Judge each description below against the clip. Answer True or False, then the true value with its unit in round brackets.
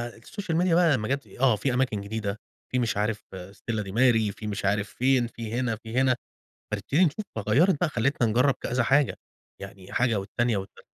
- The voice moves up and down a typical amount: True (3.8 semitones)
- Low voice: True (115 Hz)